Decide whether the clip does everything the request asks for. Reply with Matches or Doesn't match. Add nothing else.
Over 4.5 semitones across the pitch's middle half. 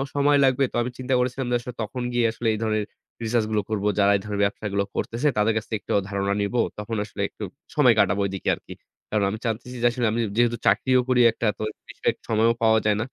Doesn't match